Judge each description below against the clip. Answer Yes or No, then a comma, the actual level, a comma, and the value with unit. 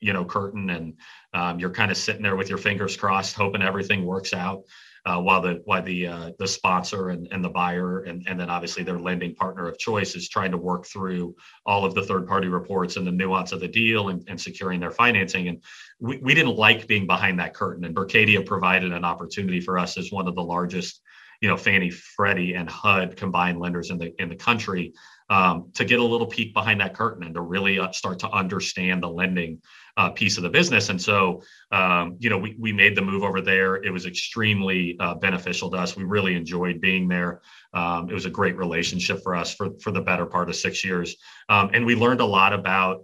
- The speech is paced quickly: Yes, fast, 230 wpm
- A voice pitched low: Yes, very low, 95 Hz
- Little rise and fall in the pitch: Yes, narrow, 1.7 semitones